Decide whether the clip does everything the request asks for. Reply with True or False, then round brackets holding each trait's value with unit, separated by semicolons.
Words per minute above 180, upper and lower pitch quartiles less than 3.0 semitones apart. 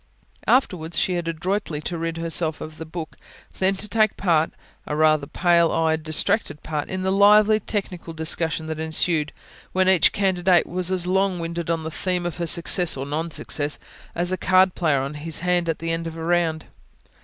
True (195 wpm; 2.6 semitones)